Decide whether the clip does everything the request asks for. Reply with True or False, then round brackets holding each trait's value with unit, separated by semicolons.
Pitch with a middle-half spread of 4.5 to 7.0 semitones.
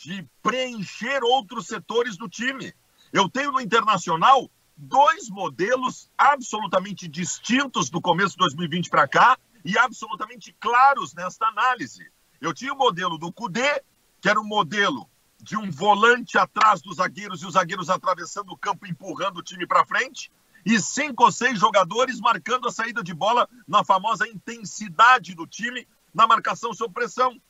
True (5.1 semitones)